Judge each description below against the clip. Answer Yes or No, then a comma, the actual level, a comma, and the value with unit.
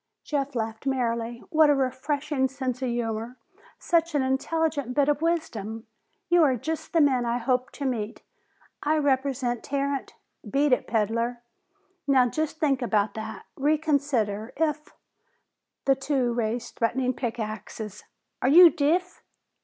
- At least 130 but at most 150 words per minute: Yes, average, 145 wpm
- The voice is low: No, very high, 265 Hz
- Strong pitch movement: No, average, 3.8 semitones